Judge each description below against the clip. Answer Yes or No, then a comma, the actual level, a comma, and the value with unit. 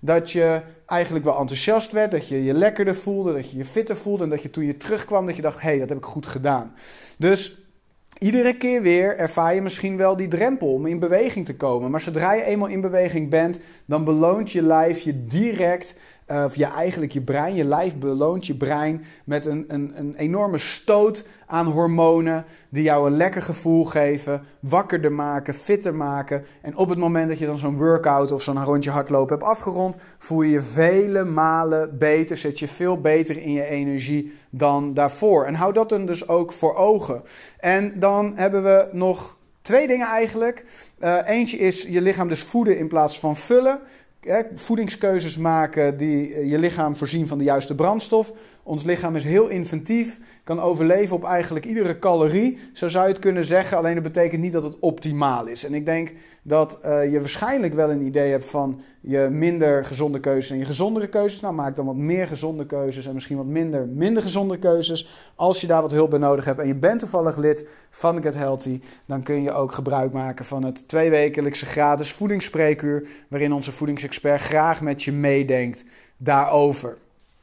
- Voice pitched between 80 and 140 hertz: No, medium, 160 Hz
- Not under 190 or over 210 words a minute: Yes, average, 195 wpm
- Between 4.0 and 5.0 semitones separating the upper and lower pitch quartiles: Yes, average, 4.3 semitones